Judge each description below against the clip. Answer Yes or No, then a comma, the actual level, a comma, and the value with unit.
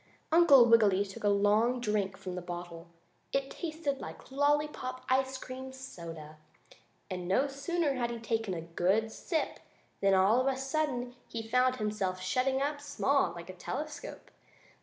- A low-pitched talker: No, high, 240 Hz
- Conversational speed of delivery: Yes, average, 160 wpm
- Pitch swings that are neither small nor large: No, wide, 6.0 semitones